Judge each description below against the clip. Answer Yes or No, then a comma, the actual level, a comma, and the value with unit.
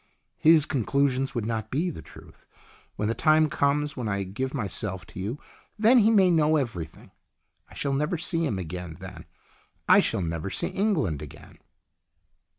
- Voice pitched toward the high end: No, low, 130 Hz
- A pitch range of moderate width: No, wide, 8.2 semitones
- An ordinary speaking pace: Yes, average, 170 wpm